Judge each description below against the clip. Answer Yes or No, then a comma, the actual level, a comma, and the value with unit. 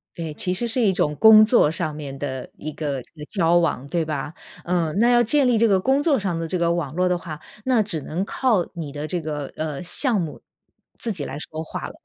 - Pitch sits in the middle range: Yes, medium, 170 Hz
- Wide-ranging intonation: Yes, wide, 5.8 semitones